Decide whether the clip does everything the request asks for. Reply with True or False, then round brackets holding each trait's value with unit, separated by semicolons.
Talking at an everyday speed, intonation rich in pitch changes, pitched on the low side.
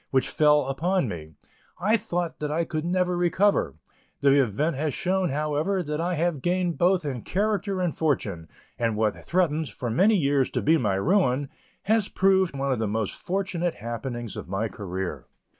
False (180 wpm; 6.6 semitones; 155 Hz)